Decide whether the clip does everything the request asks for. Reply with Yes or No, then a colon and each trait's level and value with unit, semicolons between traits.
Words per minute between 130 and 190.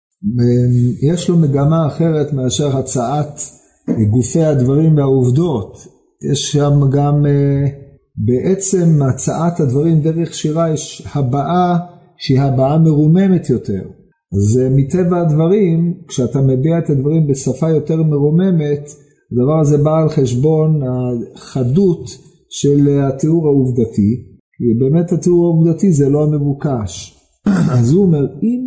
No: average, 110 wpm